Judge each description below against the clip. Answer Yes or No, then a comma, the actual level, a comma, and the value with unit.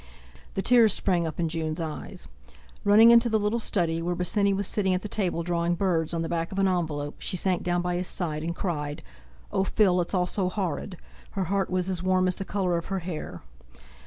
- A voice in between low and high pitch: Yes, medium, 180 Hz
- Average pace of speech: No, fast, 220 wpm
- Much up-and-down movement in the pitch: No, narrow, 2.5 semitones